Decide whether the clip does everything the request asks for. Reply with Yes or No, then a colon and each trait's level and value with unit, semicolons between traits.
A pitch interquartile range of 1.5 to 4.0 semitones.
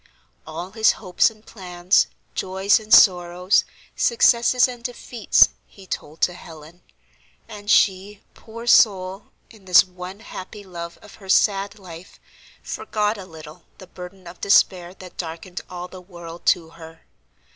Yes: average, 3.0 semitones